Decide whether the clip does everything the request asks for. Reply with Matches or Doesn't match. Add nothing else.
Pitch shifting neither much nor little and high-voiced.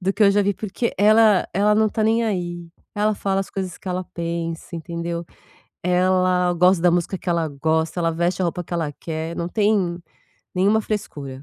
Doesn't match